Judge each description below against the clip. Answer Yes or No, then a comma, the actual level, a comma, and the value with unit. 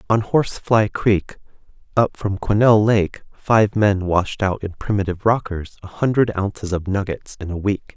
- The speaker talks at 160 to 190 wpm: Yes, average, 175 wpm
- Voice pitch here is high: No, low, 100 Hz